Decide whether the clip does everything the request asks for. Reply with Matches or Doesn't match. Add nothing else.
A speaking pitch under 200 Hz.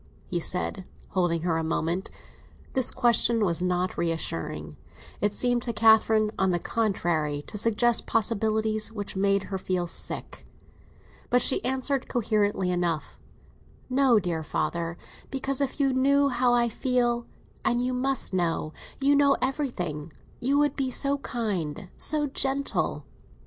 Doesn't match